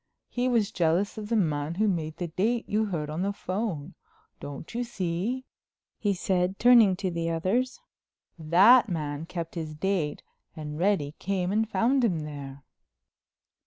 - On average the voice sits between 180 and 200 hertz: Yes, medium, 185 Hz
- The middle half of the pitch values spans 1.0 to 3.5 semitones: No, average, 5.2 semitones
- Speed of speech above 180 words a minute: No, average, 160 wpm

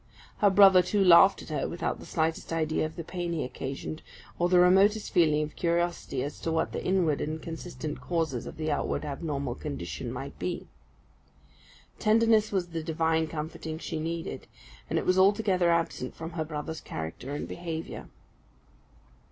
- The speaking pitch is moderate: Yes, medium, 165 Hz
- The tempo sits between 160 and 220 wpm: Yes, average, 170 wpm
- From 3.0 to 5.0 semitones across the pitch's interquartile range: No, narrow, 2.6 semitones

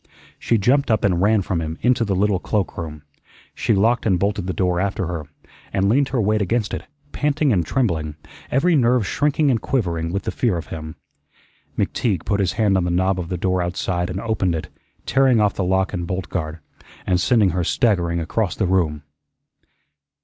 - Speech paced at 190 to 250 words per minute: Yes, average, 195 wpm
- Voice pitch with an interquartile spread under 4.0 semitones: No, average, 4.3 semitones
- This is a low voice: Yes, very low, 95 Hz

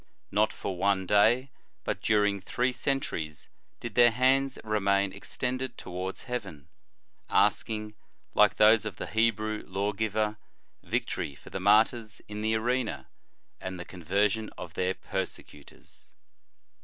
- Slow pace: Yes, slow, 130 wpm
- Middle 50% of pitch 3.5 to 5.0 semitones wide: No, average, 2.9 semitones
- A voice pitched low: Yes, low, 105 Hz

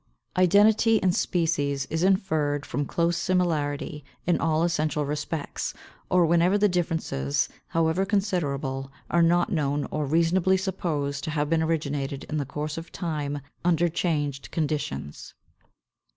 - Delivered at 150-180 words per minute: No, slow, 135 wpm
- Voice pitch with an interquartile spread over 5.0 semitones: No, average, 3.3 semitones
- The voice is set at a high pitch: No, medium, 160 Hz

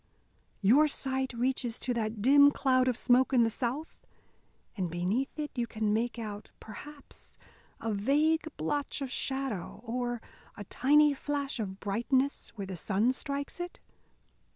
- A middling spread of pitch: Yes, average, 4.3 semitones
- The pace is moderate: Yes, average, 150 wpm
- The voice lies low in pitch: No, very high, 250 Hz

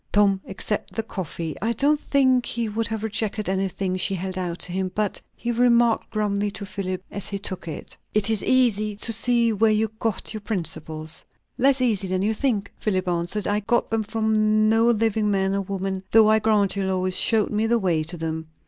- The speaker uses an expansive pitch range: No, average, 2.8 semitones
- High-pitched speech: Yes, high, 210 Hz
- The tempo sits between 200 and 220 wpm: Yes, fast, 205 wpm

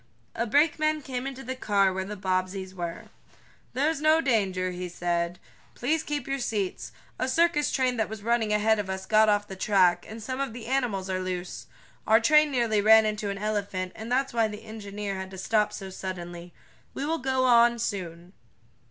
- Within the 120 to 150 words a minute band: No, average, 195 wpm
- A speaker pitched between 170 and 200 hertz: No, high, 215 Hz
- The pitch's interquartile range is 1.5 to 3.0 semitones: No, average, 5.1 semitones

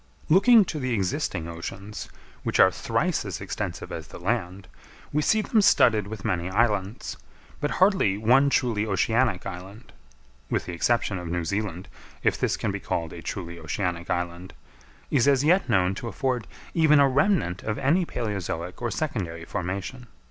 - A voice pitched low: Yes, low, 105 Hz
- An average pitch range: No, wide, 6.8 semitones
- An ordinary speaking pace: Yes, average, 165 wpm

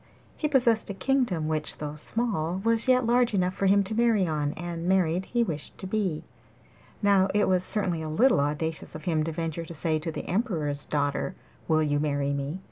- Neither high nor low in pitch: Yes, medium, 175 Hz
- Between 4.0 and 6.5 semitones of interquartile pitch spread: Yes, average, 5.3 semitones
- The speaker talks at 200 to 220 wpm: Yes, fast, 205 wpm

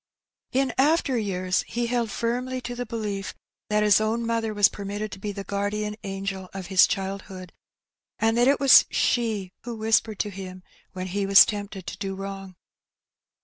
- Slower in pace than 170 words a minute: No, average, 180 wpm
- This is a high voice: Yes, high, 205 Hz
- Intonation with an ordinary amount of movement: Yes, average, 3.0 semitones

